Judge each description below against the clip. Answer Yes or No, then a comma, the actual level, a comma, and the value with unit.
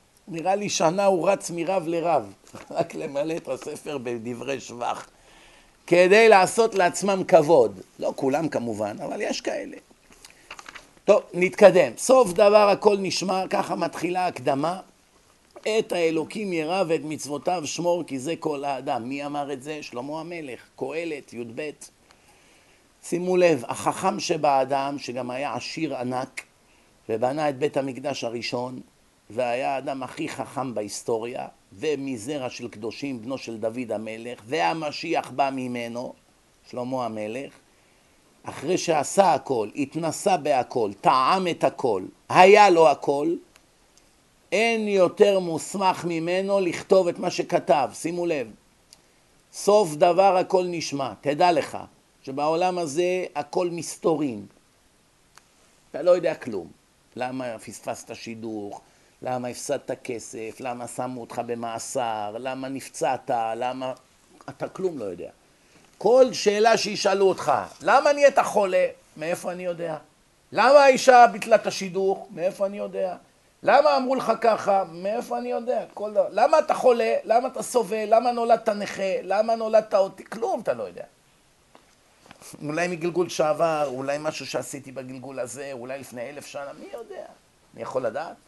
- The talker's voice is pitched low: No, medium, 165 Hz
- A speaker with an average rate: Yes, average, 130 wpm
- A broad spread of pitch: Yes, wide, 6.8 semitones